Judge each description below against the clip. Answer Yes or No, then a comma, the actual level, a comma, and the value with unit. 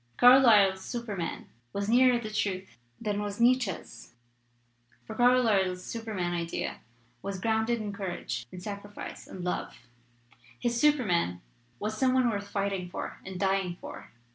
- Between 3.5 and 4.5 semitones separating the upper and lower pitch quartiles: Yes, average, 4.0 semitones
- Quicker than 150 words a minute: No, average, 140 wpm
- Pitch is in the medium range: No, high, 205 Hz